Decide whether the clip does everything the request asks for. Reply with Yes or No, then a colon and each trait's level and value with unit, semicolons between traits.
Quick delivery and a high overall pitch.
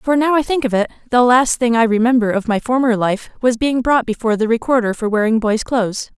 Yes: fast, 240 wpm; high, 235 Hz